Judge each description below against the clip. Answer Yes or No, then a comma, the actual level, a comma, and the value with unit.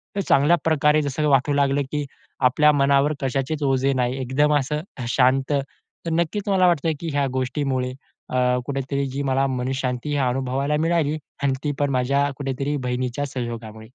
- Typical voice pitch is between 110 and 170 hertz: Yes, medium, 140 Hz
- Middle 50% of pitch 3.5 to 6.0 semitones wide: No, narrow, 2.4 semitones